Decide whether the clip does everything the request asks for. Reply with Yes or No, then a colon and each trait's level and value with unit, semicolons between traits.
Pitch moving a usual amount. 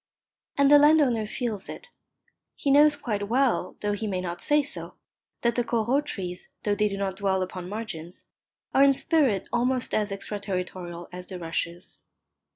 No: wide, 6.0 semitones